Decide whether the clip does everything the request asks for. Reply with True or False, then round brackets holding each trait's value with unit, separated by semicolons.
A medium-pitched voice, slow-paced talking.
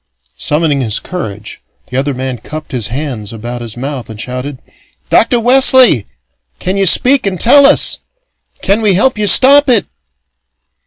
False (150 Hz; 155 wpm)